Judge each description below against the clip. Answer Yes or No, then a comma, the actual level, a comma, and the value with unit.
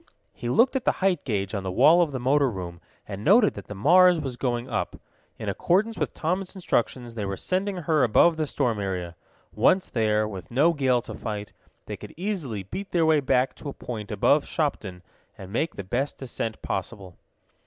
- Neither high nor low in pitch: No, low, 130 Hz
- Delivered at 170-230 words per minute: Yes, average, 200 wpm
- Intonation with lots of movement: Yes, wide, 8.1 semitones